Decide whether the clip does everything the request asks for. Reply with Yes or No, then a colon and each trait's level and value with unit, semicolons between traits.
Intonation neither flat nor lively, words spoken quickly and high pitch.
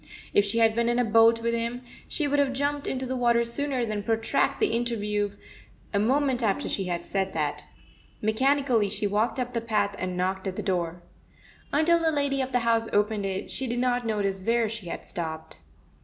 Yes: average, 3.7 semitones; fast, 210 wpm; high, 230 Hz